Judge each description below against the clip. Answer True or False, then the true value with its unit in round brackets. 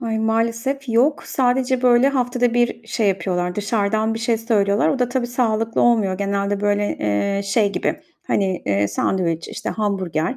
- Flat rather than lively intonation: False (3.4 semitones)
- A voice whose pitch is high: True (220 Hz)